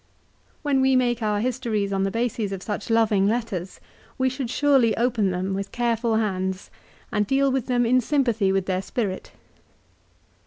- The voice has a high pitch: Yes, high, 225 Hz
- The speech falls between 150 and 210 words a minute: Yes, average, 165 wpm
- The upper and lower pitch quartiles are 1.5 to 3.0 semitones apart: No, average, 4.0 semitones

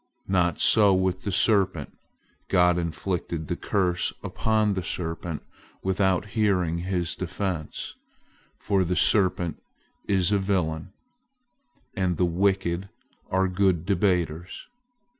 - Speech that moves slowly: Yes, slow, 110 wpm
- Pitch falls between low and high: No, very low, 90 Hz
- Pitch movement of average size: No, narrow, 2.1 semitones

